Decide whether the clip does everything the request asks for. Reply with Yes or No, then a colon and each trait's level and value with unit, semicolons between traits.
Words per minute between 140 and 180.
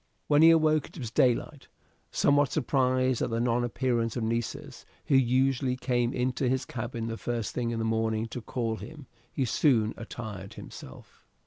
Yes: average, 175 wpm